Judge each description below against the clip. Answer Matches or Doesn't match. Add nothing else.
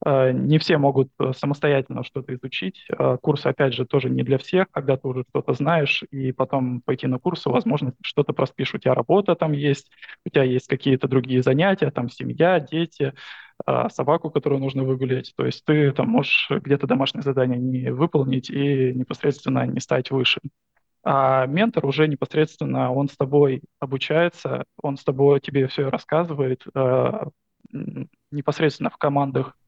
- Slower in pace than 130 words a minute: Doesn't match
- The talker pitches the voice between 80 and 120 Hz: Doesn't match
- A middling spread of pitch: Doesn't match